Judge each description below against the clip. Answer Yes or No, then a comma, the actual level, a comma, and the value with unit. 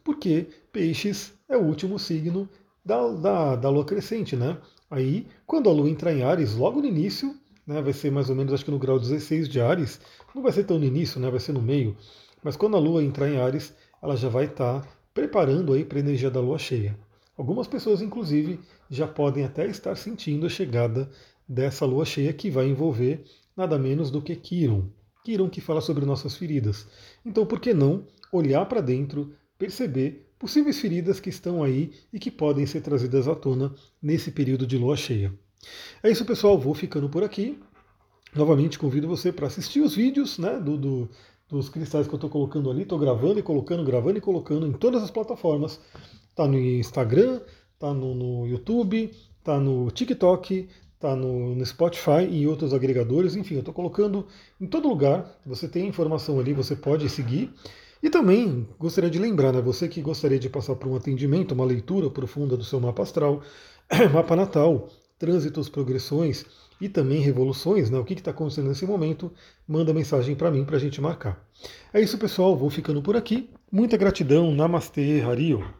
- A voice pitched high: No, medium, 150 Hz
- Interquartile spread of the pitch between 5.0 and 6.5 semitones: Yes, average, 5.3 semitones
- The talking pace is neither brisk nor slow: No, fast, 190 wpm